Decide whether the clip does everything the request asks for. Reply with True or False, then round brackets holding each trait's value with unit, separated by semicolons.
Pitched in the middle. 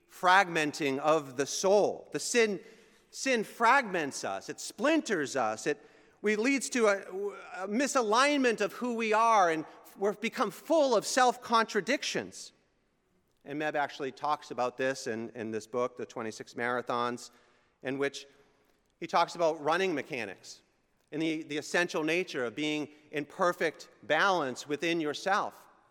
True (160 Hz)